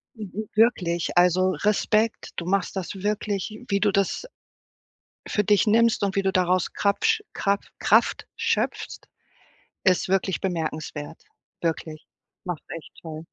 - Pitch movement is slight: No, average, 3.0 semitones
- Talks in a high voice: Yes, high, 195 Hz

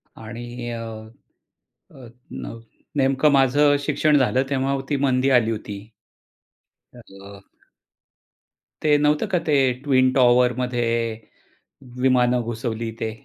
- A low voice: Yes, low, 125 Hz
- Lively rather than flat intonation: No, average, 2.9 semitones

